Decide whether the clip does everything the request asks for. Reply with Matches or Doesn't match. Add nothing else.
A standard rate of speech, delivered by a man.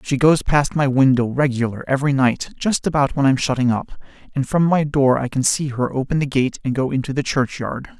Doesn't match